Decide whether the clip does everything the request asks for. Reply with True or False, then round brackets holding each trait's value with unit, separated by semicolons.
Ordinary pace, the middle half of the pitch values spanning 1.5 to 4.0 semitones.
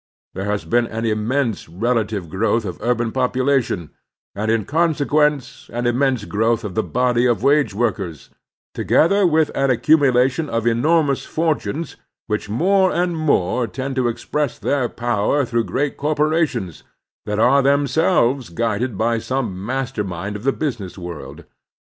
False (150 wpm; 4.6 semitones)